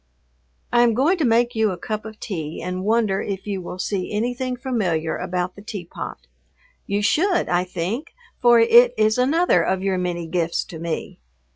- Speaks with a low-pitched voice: No, high, 205 Hz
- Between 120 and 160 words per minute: No, average, 180 wpm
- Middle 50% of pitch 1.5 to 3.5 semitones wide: No, average, 4.9 semitones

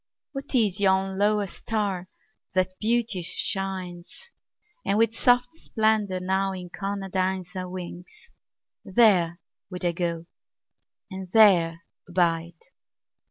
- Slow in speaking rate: Yes, slow, 105 wpm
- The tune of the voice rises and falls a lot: No, average, 2.7 semitones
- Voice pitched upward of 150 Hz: Yes, high, 190 Hz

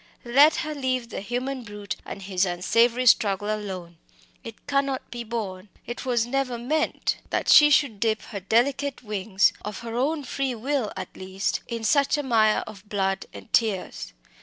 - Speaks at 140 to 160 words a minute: No, average, 170 wpm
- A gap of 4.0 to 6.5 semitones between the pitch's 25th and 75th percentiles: Yes, average, 4.5 semitones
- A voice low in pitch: No, high, 230 Hz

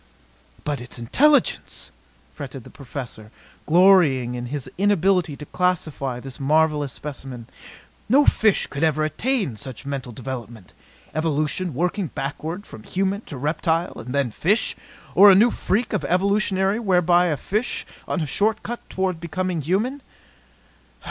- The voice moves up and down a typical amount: No, wide, 5.9 semitones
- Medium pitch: Yes, medium, 160 Hz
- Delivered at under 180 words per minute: Yes, average, 140 wpm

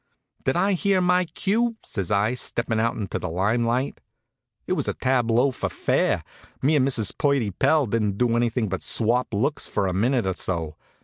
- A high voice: No, low, 120 Hz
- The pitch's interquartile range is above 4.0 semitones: Yes, average, 5.1 semitones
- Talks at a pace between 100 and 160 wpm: No, average, 190 wpm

